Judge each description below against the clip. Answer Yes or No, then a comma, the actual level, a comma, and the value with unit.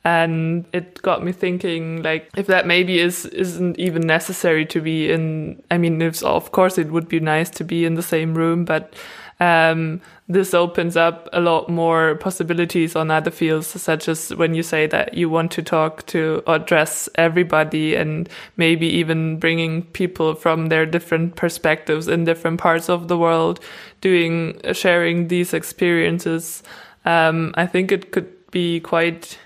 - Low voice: No, medium, 165 Hz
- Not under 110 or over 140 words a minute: No, average, 170 wpm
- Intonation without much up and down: Yes, narrow, 1.3 semitones